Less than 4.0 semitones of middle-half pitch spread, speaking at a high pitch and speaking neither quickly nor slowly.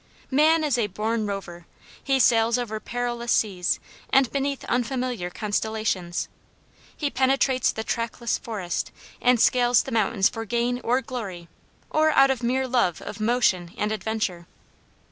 Yes: average, 3.4 semitones; high, 235 Hz; average, 145 wpm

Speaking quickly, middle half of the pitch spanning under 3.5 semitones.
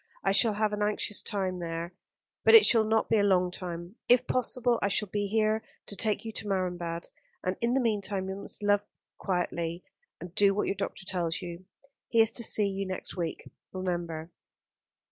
No: average, 195 wpm; average, 3.1 semitones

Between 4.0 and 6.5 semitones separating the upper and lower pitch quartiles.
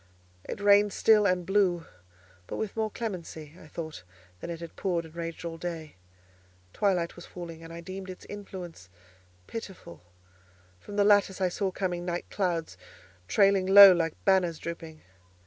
No: average, 3.0 semitones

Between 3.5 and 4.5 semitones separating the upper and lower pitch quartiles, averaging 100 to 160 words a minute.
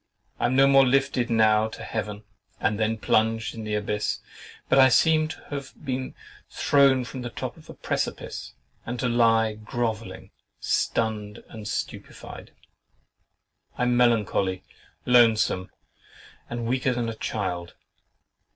No: average, 2.9 semitones; average, 140 wpm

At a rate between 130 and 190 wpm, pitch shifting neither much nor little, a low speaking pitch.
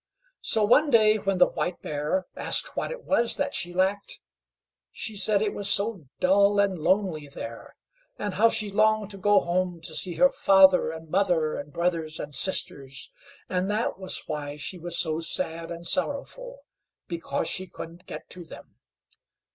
No: average, 170 wpm; average, 3.8 semitones; medium, 185 Hz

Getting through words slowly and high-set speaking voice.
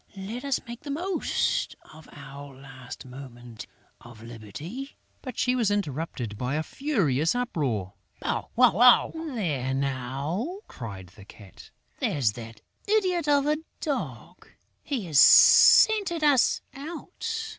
No: slow, 130 wpm; medium, 160 Hz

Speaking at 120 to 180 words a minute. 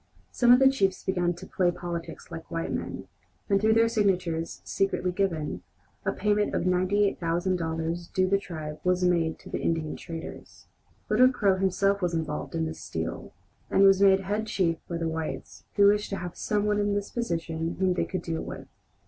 No: average, 190 wpm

